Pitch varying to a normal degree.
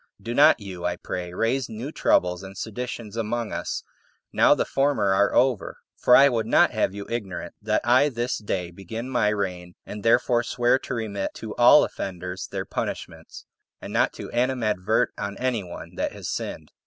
Yes: average, 4.1 semitones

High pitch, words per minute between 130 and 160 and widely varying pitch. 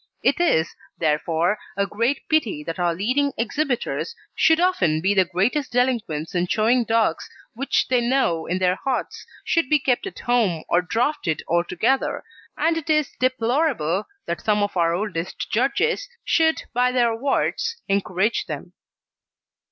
Yes: high, 230 Hz; average, 150 wpm; wide, 7.2 semitones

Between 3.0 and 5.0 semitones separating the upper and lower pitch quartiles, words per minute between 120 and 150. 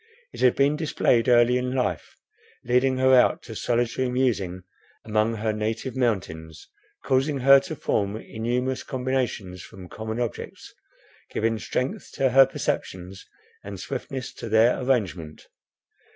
Yes: average, 3.4 semitones; slow, 135 wpm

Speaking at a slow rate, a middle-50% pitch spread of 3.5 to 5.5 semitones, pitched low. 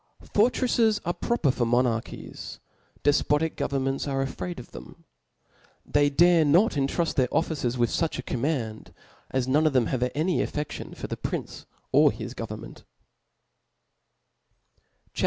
No: slow, 130 wpm; average, 4.3 semitones; medium, 145 Hz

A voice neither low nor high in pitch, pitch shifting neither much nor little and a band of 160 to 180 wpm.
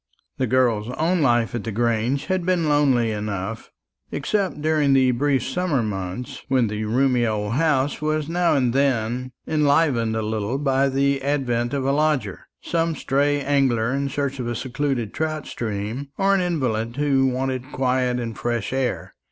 No: low, 130 Hz; average, 3.6 semitones; average, 170 wpm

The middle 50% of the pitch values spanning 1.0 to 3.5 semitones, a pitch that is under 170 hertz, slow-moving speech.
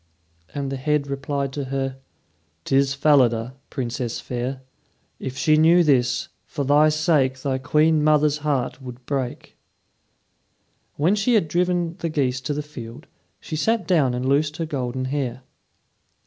No: average, 2.9 semitones; medium, 140 Hz; average, 150 wpm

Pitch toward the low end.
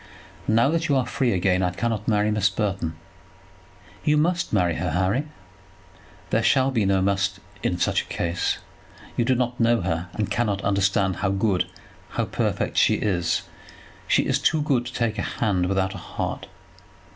Yes: low, 105 Hz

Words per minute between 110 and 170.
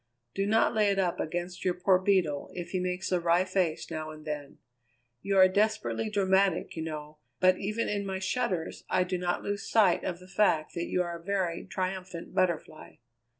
No: average, 195 wpm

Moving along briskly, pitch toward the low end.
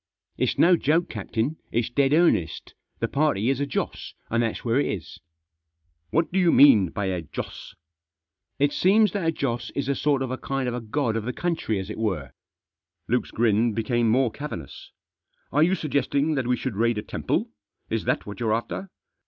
Yes: fast, 210 wpm; low, 120 Hz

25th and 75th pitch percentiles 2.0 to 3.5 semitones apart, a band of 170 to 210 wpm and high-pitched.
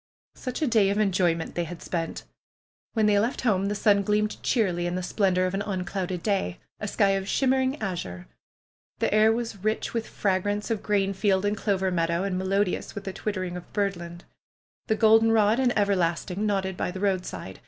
Yes: narrow, 2.6 semitones; average, 185 wpm; high, 195 Hz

